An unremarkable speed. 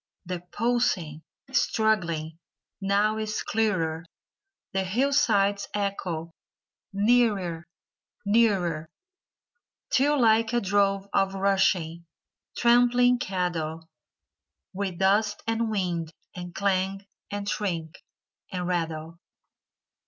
No: slow, 85 wpm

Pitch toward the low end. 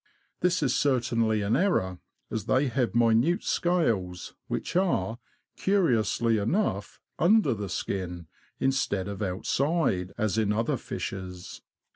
Yes: low, 115 Hz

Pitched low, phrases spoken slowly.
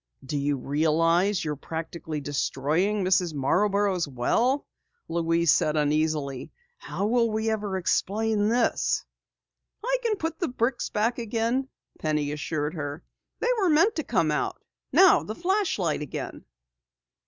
No: medium, 185 Hz; slow, 130 wpm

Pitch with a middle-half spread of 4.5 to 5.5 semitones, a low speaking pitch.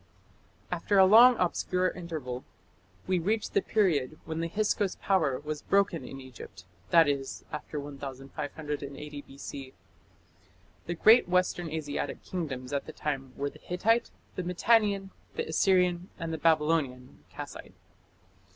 No: average, 4.8 semitones; medium, 160 Hz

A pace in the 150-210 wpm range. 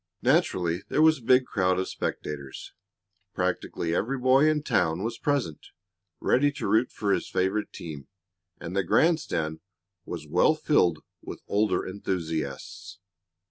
No: average, 140 wpm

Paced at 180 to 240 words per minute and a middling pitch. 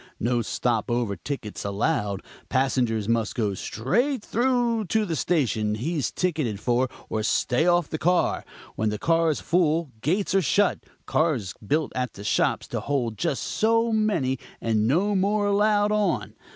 No: average, 155 wpm; medium, 145 Hz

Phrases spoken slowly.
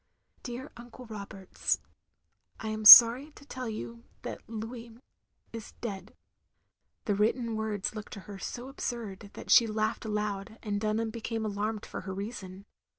No: average, 155 wpm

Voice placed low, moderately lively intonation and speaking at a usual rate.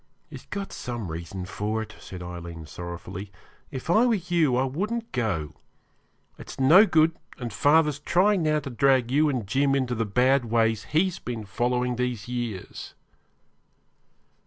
No: low, 125 Hz; wide, 6.2 semitones; average, 155 wpm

